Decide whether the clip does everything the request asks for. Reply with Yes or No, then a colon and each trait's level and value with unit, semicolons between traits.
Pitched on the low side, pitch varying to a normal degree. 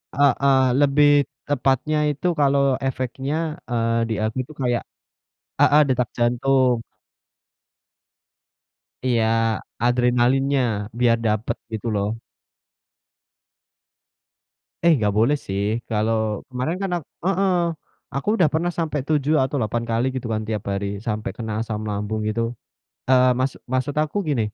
Yes: low, 125 Hz; average, 4.1 semitones